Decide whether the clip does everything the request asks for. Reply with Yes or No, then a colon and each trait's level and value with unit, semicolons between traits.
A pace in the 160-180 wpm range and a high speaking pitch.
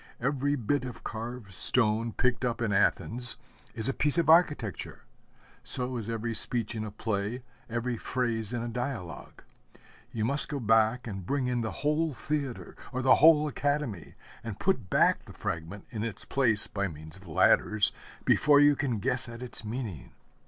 No: average, 175 wpm; low, 120 Hz